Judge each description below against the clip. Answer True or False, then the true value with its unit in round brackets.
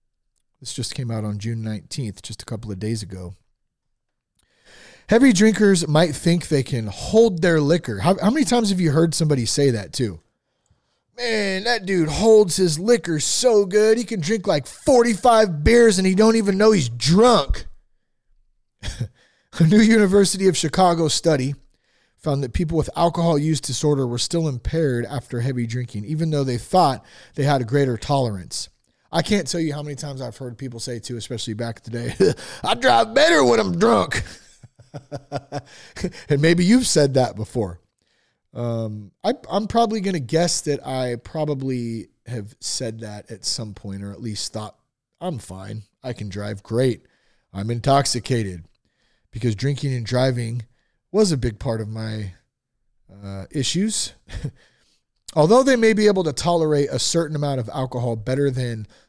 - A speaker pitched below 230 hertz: True (140 Hz)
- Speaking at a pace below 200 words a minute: True (170 wpm)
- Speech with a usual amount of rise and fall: False (6.8 semitones)